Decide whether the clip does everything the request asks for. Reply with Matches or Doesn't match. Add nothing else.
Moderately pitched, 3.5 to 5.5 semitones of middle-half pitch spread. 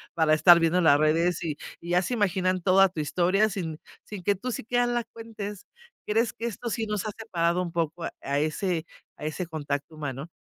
Matches